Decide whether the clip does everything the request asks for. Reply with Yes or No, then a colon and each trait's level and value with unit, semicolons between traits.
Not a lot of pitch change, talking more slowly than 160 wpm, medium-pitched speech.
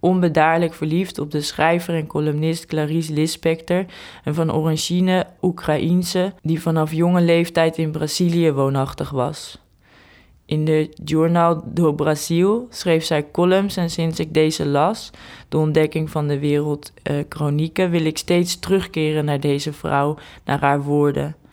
Yes: narrow, 2.1 semitones; average, 140 wpm; medium, 160 Hz